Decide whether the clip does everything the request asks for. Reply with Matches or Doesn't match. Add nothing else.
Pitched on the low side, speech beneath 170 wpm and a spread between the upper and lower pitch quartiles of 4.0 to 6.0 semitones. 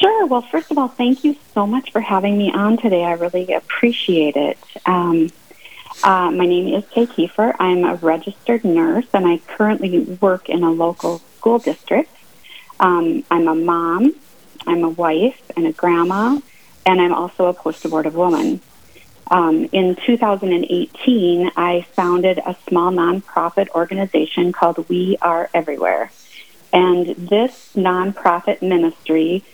Doesn't match